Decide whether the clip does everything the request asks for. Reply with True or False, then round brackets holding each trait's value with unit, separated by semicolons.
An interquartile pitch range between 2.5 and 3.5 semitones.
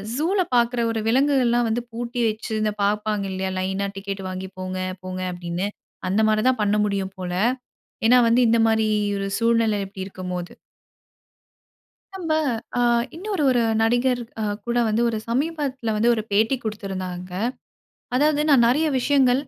False (4.1 semitones)